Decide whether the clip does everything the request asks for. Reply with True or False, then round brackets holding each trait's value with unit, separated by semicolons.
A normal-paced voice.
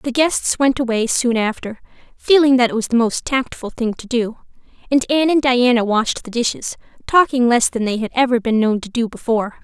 False (210 wpm)